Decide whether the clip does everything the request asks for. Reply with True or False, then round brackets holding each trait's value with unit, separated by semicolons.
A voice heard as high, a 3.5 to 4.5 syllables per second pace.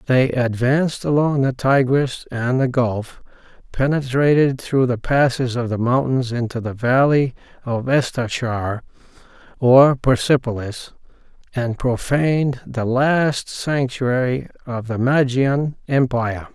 False (130 Hz; 3.9 syllables/s)